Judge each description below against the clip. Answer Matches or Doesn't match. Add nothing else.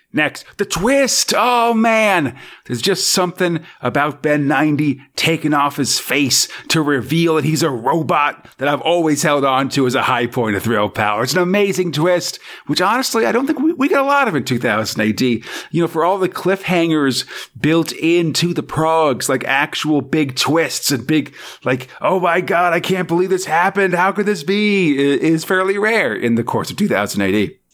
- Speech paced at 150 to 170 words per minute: Doesn't match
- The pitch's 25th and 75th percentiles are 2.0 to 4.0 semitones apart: Doesn't match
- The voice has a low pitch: Doesn't match